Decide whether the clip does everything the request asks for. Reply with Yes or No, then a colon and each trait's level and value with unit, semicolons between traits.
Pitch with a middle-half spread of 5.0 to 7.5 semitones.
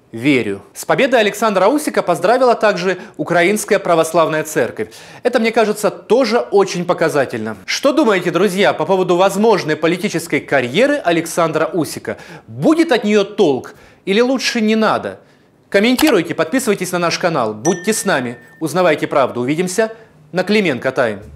Yes: average, 5.3 semitones